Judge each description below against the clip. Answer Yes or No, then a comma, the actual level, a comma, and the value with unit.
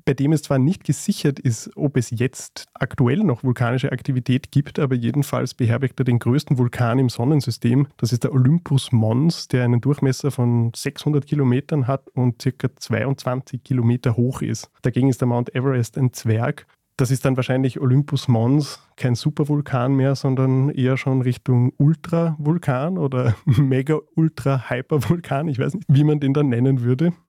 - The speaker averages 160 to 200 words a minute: Yes, average, 165 wpm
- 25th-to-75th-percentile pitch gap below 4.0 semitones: Yes, narrow, 2.5 semitones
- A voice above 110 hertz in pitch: Yes, low, 135 Hz